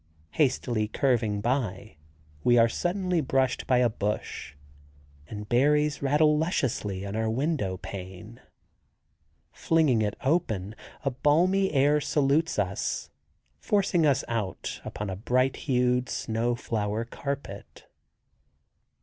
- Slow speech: Yes, slow, 115 wpm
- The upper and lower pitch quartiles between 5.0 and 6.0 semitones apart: Yes, wide, 5.6 semitones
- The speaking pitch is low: Yes, low, 125 Hz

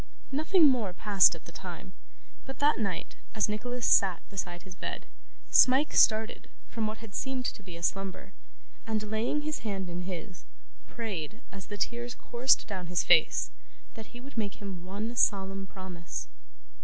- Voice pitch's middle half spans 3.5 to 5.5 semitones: Yes, average, 4.3 semitones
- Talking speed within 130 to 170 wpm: Yes, average, 165 wpm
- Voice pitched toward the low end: No, high, 210 Hz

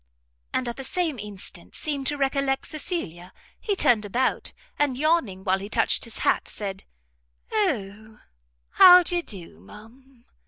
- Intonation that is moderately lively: No, wide, 6.5 semitones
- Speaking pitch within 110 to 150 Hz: No, very high, 255 Hz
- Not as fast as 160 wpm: Yes, average, 145 wpm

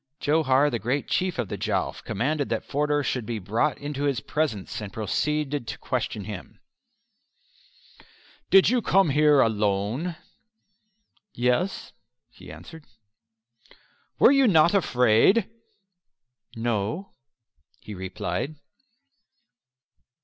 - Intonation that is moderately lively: No, wide, 5.8 semitones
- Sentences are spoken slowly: Yes, slow, 110 wpm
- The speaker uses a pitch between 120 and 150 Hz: Yes, medium, 140 Hz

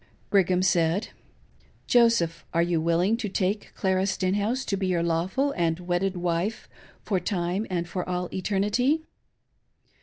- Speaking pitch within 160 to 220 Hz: Yes, medium, 185 Hz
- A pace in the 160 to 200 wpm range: No, average, 145 wpm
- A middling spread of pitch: Yes, average, 3.0 semitones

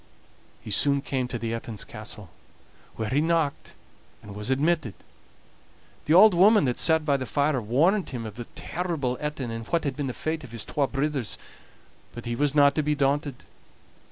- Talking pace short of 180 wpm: No, average, 185 wpm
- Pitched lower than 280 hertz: Yes, medium, 140 Hz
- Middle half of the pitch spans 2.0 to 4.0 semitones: No, average, 4.5 semitones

